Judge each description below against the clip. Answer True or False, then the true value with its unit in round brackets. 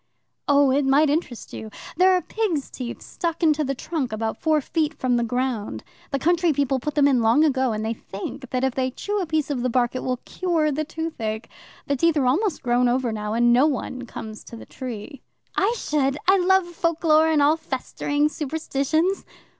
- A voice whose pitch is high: True (280 Hz)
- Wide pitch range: False (4.2 semitones)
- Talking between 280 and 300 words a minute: False (205 wpm)